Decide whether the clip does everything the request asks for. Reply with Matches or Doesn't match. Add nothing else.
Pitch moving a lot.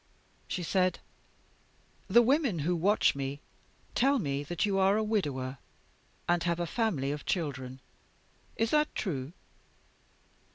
Matches